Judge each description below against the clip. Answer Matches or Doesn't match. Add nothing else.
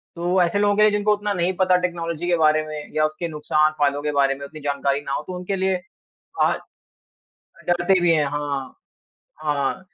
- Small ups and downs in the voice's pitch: Doesn't match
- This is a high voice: Doesn't match